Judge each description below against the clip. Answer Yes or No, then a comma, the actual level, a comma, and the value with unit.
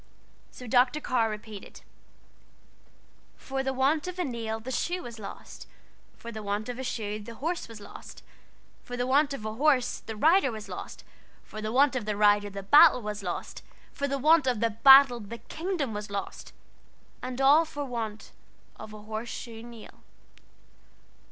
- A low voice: No, high, 240 Hz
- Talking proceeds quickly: No, average, 175 wpm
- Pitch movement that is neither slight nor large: Yes, average, 4.2 semitones